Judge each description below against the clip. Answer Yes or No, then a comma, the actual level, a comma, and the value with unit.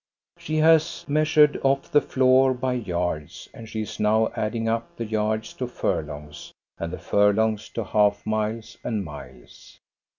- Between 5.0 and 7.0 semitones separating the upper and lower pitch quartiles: No, average, 3.7 semitones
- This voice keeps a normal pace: Yes, average, 160 wpm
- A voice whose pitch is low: Yes, low, 110 Hz